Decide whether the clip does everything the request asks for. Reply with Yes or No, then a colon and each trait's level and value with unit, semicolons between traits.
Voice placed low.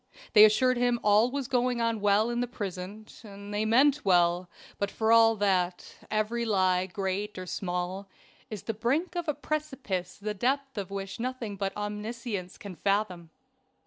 No: high, 210 Hz